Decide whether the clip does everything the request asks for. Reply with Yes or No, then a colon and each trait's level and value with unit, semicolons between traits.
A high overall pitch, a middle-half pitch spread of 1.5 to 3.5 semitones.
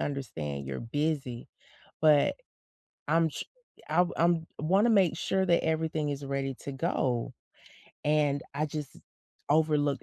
No: medium, 150 Hz; average, 2.8 semitones